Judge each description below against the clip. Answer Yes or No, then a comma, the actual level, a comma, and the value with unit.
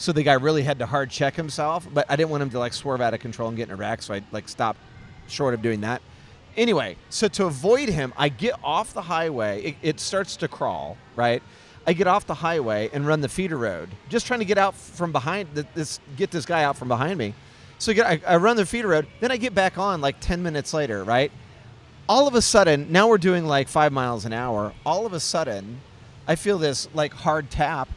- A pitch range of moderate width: No, wide, 6.7 semitones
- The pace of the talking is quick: Yes, fast, 245 wpm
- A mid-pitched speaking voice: Yes, medium, 145 Hz